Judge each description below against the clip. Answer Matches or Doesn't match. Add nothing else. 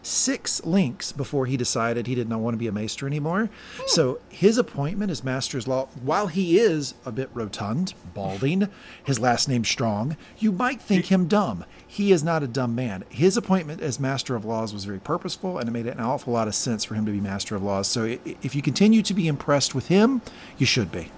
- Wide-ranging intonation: Matches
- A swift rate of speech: Matches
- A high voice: Doesn't match